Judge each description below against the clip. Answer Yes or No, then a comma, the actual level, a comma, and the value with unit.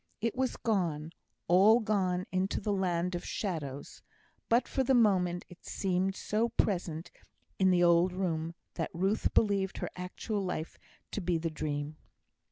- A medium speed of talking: Yes, average, 155 wpm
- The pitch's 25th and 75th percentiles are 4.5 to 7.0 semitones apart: No, average, 3.2 semitones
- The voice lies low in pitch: No, medium, 185 Hz